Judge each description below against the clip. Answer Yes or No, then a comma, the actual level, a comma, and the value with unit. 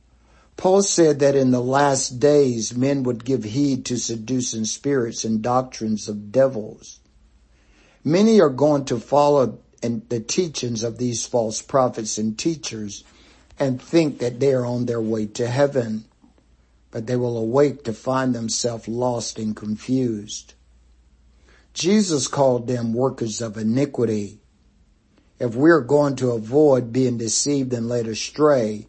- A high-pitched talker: No, low, 120 Hz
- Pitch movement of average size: Yes, average, 3.9 semitones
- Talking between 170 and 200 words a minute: No, average, 140 wpm